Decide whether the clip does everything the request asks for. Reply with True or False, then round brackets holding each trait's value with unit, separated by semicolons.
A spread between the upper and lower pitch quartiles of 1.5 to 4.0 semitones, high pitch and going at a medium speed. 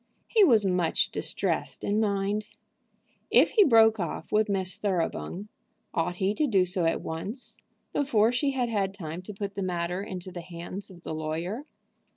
True (3.5 semitones; 195 Hz; 175 wpm)